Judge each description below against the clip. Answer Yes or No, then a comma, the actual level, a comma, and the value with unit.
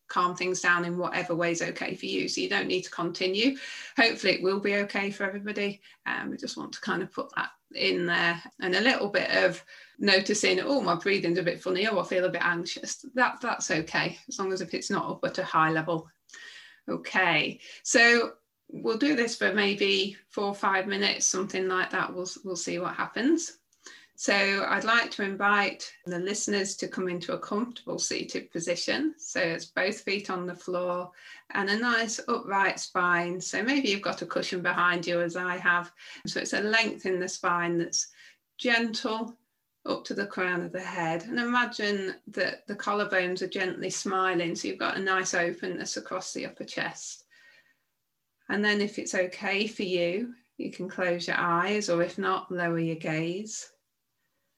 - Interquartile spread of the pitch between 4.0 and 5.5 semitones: No, average, 3.5 semitones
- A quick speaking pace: No, average, 190 wpm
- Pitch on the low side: No, high, 190 Hz